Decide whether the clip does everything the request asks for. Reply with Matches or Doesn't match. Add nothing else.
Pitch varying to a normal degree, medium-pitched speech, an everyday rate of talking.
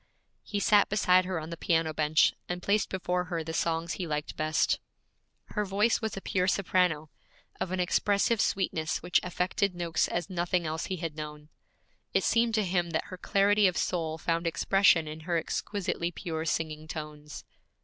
Matches